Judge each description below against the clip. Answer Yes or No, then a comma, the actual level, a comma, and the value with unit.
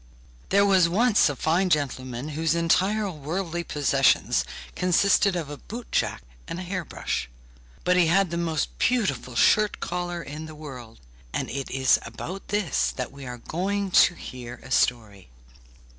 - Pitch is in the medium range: Yes, medium, 165 Hz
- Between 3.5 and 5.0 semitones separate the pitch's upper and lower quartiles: No, wide, 5.4 semitones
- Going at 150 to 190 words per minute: Yes, average, 160 wpm